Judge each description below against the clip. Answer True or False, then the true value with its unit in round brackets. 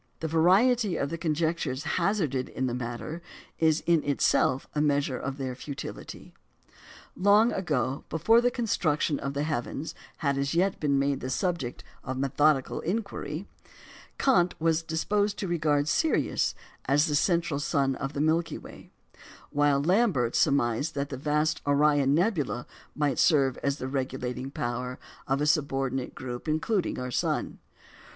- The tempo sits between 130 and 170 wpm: True (150 wpm)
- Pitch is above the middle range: False (145 Hz)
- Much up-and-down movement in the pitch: False (3.7 semitones)